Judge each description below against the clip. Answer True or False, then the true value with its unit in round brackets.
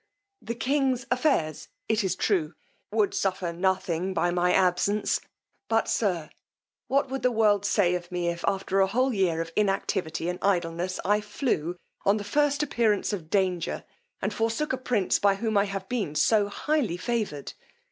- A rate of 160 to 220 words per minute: True (165 wpm)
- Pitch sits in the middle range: False (200 Hz)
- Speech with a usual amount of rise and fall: True (4.1 semitones)